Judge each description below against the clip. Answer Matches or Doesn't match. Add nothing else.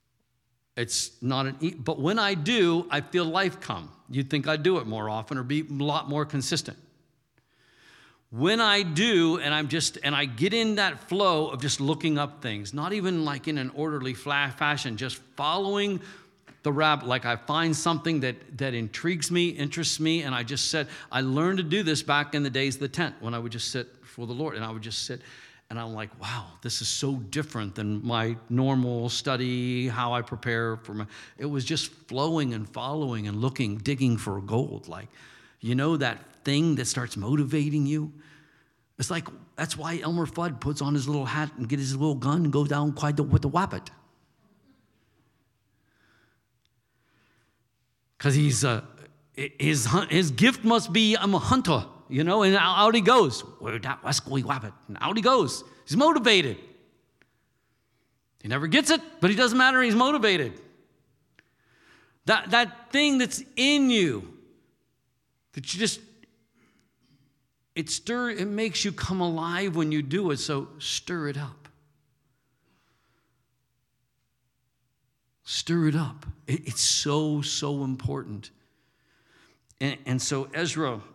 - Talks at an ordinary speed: Matches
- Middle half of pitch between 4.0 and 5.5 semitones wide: Matches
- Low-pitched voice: Doesn't match